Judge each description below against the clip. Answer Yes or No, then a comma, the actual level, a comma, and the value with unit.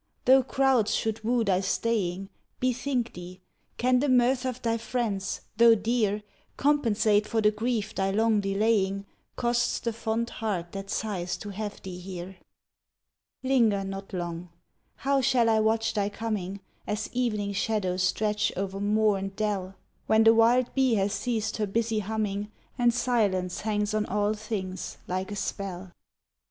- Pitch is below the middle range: No, high, 215 Hz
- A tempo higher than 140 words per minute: Yes, average, 155 wpm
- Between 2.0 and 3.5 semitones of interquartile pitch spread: Yes, average, 2.8 semitones